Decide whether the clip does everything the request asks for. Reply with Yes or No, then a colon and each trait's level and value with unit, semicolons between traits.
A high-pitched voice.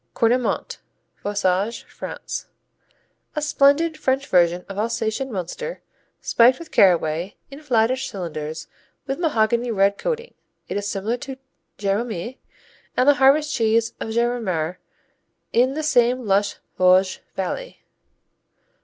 Yes: high, 230 Hz